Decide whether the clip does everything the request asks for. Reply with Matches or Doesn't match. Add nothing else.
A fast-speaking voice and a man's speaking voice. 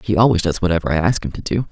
Matches